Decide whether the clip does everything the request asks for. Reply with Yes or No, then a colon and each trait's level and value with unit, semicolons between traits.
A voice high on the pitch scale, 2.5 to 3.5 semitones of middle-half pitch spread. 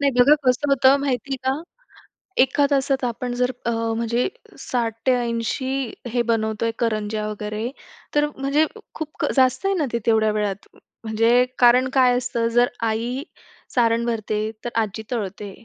Yes: high, 240 Hz; average, 2.9 semitones